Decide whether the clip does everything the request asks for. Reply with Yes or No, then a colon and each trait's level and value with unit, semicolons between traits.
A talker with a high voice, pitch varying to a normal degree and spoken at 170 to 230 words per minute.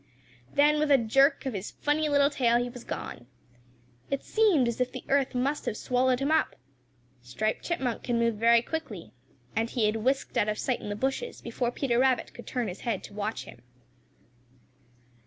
Yes: high, 245 Hz; average, 3.7 semitones; average, 195 wpm